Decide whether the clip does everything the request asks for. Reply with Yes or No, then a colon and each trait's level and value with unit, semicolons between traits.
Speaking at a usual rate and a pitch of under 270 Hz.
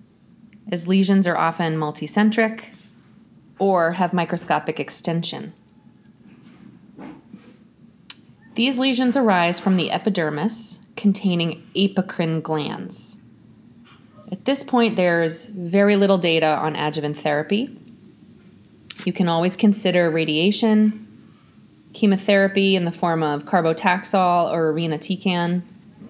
No: slow, 95 wpm; medium, 185 Hz